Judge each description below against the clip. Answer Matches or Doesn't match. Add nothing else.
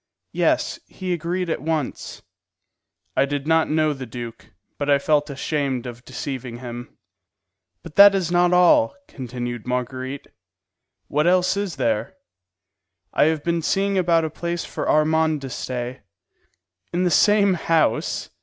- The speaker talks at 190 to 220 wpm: Doesn't match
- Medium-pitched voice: Matches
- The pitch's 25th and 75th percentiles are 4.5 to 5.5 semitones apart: Matches